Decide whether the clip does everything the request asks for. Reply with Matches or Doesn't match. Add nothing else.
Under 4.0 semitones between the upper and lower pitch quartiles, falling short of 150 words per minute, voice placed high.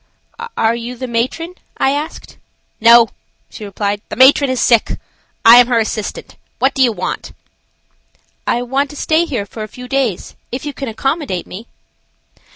Doesn't match